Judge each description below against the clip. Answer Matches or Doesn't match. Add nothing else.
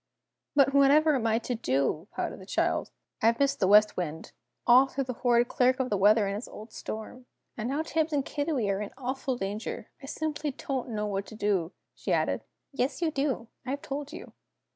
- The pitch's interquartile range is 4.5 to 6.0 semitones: Matches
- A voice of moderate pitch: Doesn't match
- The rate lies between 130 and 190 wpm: Doesn't match